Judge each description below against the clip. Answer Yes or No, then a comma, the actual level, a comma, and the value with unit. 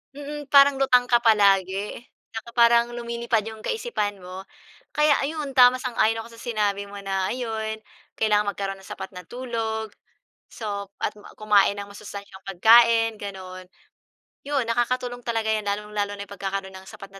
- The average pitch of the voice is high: Yes, high, 220 Hz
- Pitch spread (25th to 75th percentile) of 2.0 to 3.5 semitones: Yes, average, 3.1 semitones